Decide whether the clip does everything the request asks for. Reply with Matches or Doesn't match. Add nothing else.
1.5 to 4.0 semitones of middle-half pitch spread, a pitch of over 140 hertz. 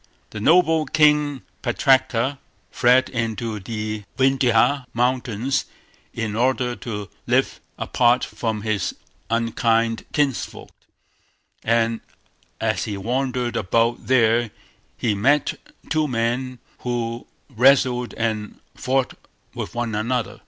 Doesn't match